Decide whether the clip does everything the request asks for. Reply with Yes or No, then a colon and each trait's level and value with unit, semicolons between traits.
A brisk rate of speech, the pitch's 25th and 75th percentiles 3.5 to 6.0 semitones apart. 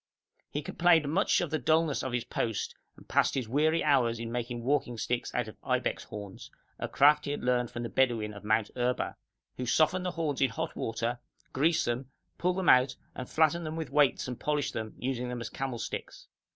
Yes: fast, 210 wpm; average, 4.1 semitones